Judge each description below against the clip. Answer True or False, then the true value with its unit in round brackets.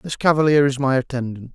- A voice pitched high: False (135 Hz)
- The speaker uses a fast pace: False (195 wpm)